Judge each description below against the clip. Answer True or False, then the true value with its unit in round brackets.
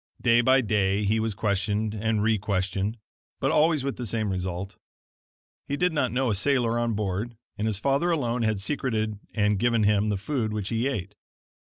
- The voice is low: True (110 Hz)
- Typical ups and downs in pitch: True (3.0 semitones)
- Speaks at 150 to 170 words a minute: False (185 wpm)